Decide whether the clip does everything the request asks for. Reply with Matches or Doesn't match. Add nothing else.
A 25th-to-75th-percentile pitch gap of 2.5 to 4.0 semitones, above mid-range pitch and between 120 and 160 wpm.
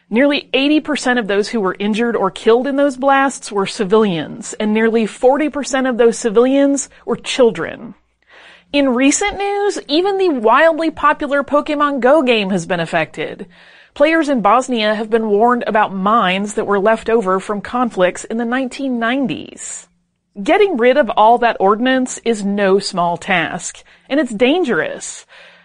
Doesn't match